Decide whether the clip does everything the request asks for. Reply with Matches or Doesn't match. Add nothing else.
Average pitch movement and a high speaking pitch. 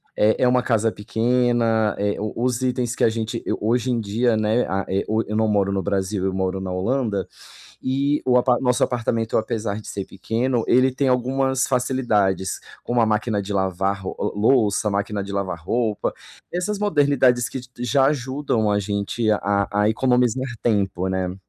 Doesn't match